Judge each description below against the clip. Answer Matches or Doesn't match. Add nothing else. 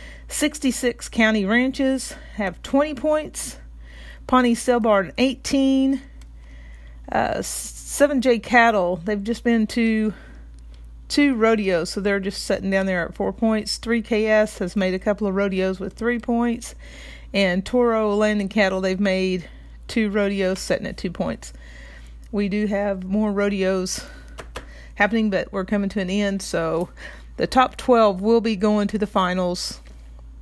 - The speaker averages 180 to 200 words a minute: Doesn't match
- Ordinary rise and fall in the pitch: Matches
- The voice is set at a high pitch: Matches